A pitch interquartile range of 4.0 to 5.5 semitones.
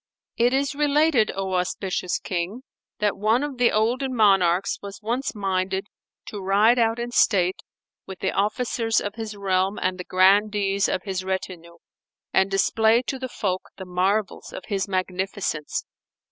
No: average, 3.3 semitones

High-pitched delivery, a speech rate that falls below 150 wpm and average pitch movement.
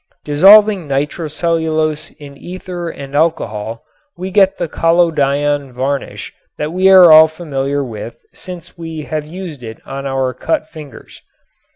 No: medium, 155 Hz; slow, 135 wpm; average, 3.6 semitones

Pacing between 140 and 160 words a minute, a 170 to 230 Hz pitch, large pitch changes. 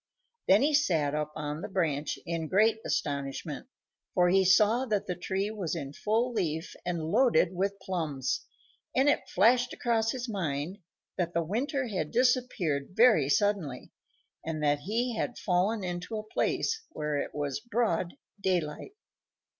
Yes: average, 155 wpm; medium, 185 Hz; wide, 6.2 semitones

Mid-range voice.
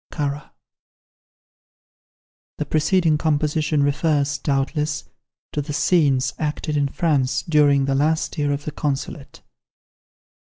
Yes: medium, 150 Hz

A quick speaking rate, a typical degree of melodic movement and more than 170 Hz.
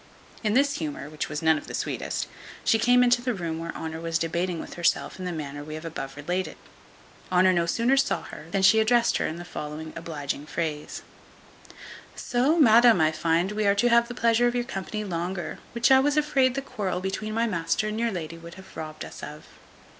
No: fast, 215 wpm; wide, 6.4 semitones; medium, 185 Hz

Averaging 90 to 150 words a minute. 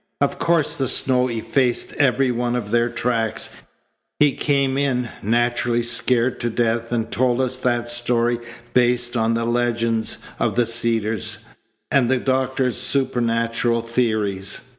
Yes: average, 140 wpm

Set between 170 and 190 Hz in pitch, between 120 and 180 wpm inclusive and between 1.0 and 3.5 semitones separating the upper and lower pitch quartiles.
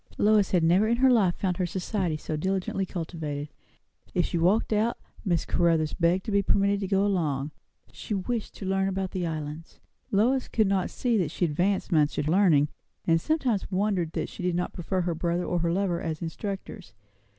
No: medium, 185 Hz; average, 195 wpm; average, 3.2 semitones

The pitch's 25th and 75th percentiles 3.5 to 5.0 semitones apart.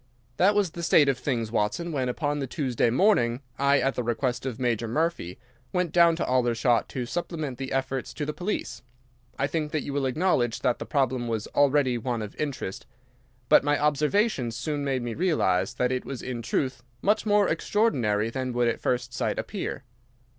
Yes: average, 4.1 semitones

